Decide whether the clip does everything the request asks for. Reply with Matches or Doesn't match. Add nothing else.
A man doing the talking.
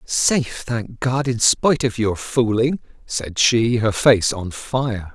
Matches